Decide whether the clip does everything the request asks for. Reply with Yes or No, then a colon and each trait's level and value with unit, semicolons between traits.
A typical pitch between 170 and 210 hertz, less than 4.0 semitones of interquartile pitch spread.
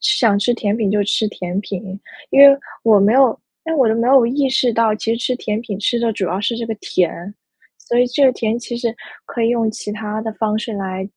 No: high, 225 Hz; narrow, 2.6 semitones